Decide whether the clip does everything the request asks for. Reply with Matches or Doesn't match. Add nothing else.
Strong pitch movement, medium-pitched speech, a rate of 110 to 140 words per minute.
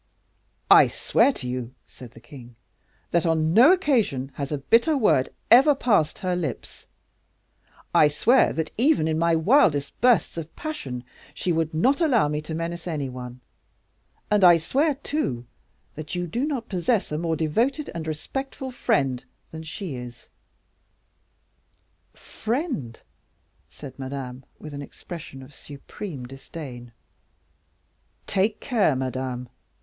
Matches